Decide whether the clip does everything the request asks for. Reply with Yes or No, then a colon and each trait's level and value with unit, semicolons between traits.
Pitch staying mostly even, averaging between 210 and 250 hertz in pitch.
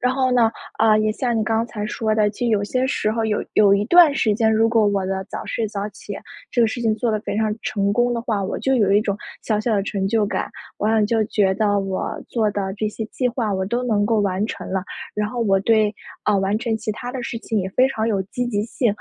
Yes: narrow, 2.3 semitones; high, 215 Hz